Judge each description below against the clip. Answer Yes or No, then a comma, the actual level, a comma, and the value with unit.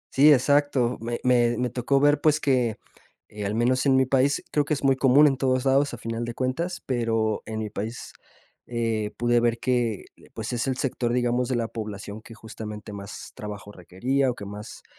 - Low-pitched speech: Yes, low, 120 Hz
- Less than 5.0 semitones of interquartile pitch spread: Yes, average, 3.2 semitones